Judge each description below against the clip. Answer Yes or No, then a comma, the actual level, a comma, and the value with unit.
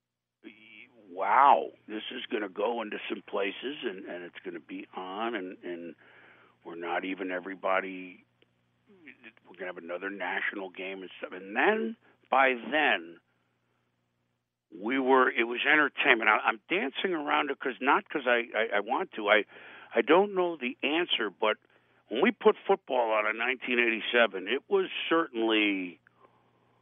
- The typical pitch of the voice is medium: No, low, 110 Hz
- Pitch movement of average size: No, wide, 7.1 semitones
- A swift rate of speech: No, average, 155 wpm